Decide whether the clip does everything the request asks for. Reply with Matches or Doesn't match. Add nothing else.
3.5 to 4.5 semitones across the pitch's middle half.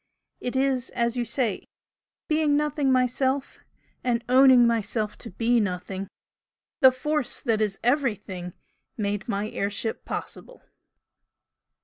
Matches